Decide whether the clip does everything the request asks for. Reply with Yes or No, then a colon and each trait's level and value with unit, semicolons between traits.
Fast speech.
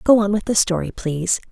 Yes: fast, 240 wpm